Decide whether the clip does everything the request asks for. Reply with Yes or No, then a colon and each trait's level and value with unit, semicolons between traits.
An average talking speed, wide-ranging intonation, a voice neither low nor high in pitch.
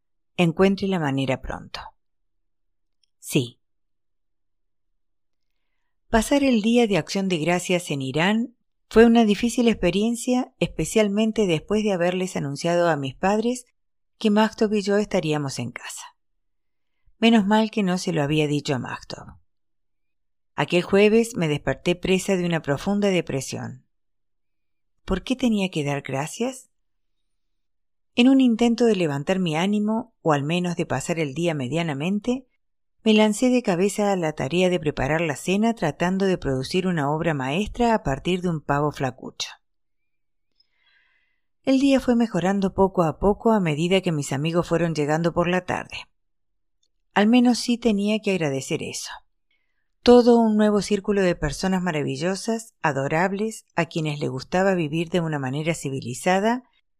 Yes: average, 145 wpm; wide, 6.8 semitones; medium, 175 Hz